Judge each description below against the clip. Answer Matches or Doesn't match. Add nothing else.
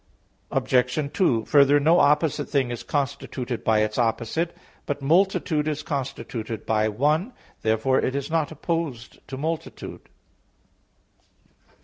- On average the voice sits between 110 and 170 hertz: Matches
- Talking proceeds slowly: Matches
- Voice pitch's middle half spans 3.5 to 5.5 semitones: Matches